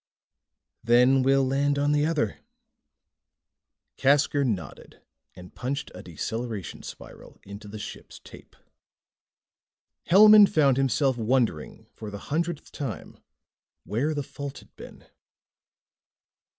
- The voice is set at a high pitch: No, low, 135 Hz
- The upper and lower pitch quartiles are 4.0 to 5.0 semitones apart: Yes, average, 4.5 semitones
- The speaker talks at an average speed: No, slow, 110 wpm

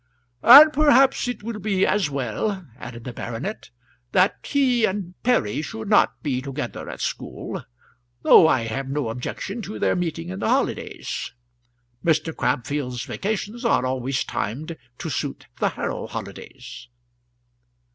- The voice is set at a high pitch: No, medium, 165 Hz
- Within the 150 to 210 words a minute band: No, average, 140 wpm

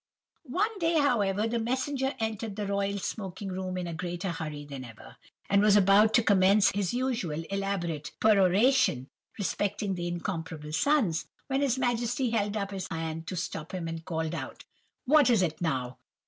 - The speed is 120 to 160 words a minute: No, average, 170 wpm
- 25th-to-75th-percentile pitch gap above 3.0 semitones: Yes, wide, 5.4 semitones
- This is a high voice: Yes, high, 195 Hz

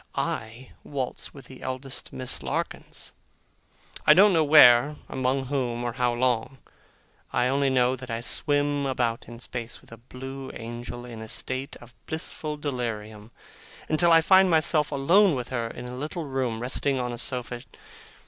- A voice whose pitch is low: Yes, low, 130 Hz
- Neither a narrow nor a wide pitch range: Yes, average, 3.0 semitones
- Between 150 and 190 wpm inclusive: Yes, average, 165 wpm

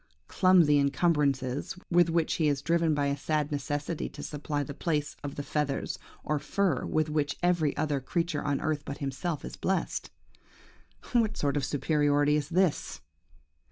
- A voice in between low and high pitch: Yes, medium, 150 Hz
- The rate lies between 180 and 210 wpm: No, average, 160 wpm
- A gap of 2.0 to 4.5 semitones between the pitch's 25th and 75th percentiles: Yes, narrow, 2.6 semitones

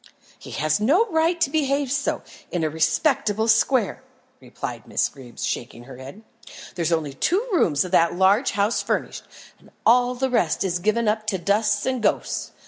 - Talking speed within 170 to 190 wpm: Yes, average, 175 wpm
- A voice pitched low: No, high, 210 Hz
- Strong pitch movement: Yes, wide, 7.5 semitones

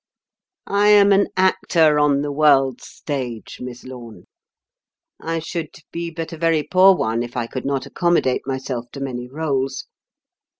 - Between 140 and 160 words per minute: Yes, average, 155 wpm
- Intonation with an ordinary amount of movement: Yes, average, 4.5 semitones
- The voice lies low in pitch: No, medium, 145 Hz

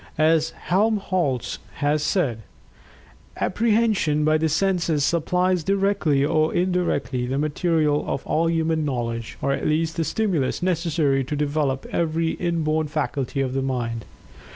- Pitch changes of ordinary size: Yes, average, 3.5 semitones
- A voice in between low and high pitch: Yes, medium, 155 Hz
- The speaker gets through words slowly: Yes, slow, 130 wpm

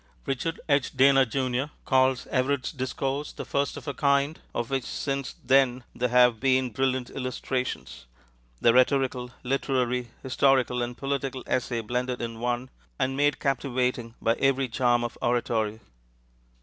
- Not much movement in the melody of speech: Yes, narrow, 1.8 semitones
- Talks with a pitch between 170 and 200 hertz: No, low, 130 Hz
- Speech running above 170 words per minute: No, average, 140 wpm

